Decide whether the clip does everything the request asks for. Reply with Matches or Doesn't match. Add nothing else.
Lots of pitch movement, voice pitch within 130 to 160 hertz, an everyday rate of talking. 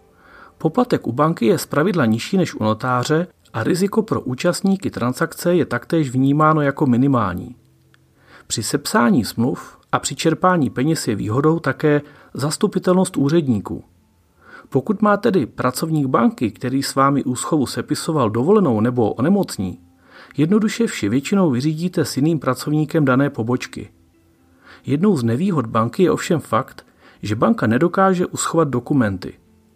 Matches